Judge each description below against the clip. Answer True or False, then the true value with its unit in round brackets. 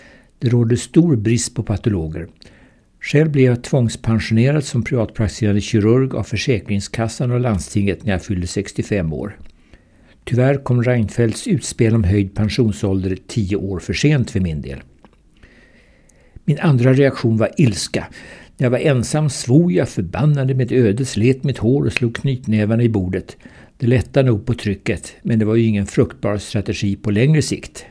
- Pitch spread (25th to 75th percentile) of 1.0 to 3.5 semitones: False (4.0 semitones)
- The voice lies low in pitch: True (115 Hz)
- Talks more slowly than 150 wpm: False (155 wpm)